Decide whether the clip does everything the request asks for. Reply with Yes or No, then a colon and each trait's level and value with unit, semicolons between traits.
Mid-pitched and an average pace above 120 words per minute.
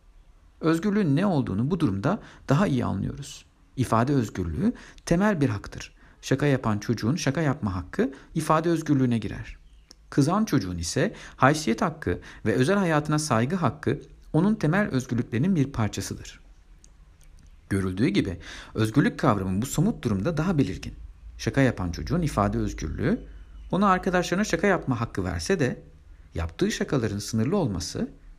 No: low, 120 Hz; average, 130 wpm